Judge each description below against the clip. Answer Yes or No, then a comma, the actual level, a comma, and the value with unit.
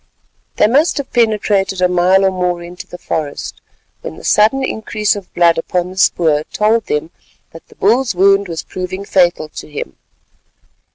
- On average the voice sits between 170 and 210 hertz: Yes, medium, 185 Hz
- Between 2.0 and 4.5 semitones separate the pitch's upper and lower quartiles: Yes, average, 3.4 semitones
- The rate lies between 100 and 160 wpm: No, average, 170 wpm